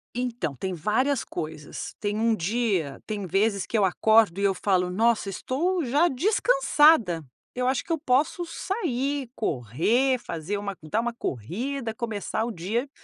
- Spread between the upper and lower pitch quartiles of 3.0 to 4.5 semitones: No, wide, 5.6 semitones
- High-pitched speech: Yes, high, 225 Hz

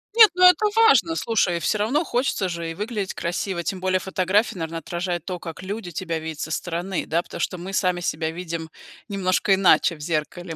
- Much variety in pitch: No, average, 3.4 semitones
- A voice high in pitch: No, medium, 180 Hz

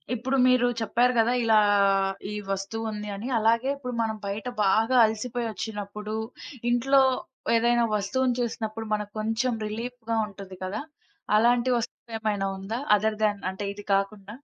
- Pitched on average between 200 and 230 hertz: Yes, high, 220 Hz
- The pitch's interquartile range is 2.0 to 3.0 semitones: Yes, narrow, 2.5 semitones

